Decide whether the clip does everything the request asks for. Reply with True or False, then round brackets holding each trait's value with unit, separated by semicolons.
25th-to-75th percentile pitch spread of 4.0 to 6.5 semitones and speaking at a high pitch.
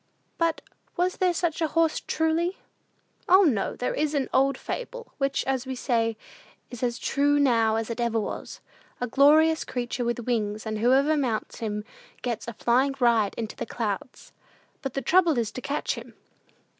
True (5.0 semitones; 260 Hz)